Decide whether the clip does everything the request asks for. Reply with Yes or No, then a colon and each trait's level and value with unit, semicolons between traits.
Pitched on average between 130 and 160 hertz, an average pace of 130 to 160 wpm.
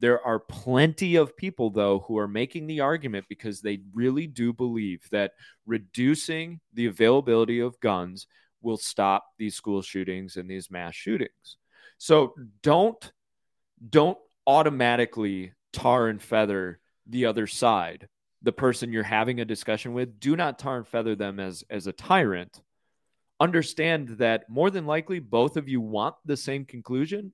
No: low, 120 Hz; average, 155 wpm